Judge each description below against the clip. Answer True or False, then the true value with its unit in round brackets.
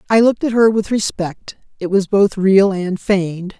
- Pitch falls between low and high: False (200 Hz)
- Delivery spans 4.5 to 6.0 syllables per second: True (4.8 syllables/s)